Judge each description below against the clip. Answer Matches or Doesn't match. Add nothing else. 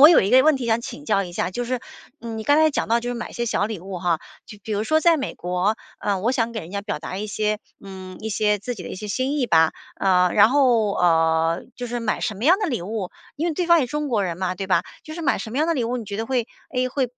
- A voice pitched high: Matches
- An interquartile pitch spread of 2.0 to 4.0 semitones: Doesn't match